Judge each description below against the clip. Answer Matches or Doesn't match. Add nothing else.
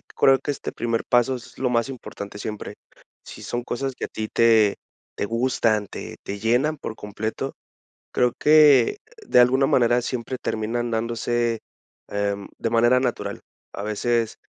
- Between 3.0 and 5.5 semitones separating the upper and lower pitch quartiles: Doesn't match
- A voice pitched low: Matches